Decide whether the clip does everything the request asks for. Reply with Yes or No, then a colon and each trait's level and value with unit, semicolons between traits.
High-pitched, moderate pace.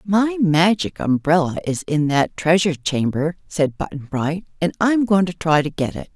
No: medium, 170 Hz; average, 185 wpm